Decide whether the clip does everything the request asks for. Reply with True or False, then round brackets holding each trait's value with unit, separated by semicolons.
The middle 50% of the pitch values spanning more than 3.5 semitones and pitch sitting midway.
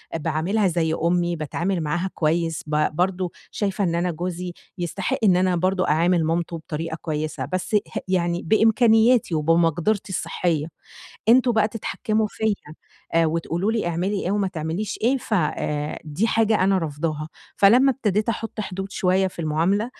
True (4.0 semitones; 180 Hz)